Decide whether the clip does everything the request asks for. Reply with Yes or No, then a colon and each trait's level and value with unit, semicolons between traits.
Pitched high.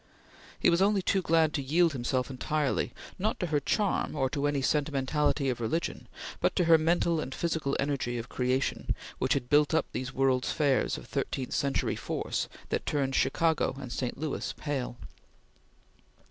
No: medium, 145 Hz